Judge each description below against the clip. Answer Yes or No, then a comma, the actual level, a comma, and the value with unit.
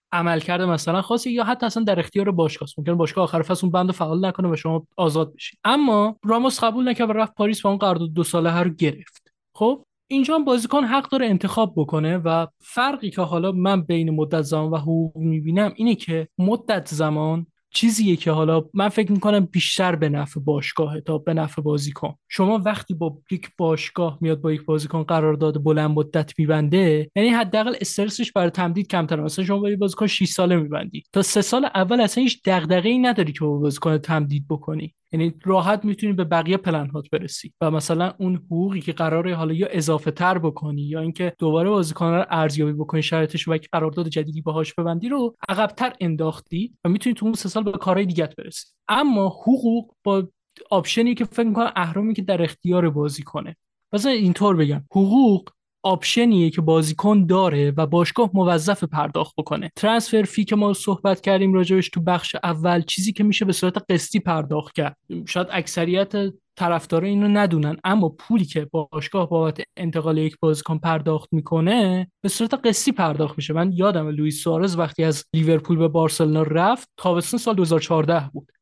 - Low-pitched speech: No, medium, 175 Hz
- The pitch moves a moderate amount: Yes, average, 4.2 semitones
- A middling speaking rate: No, fast, 180 wpm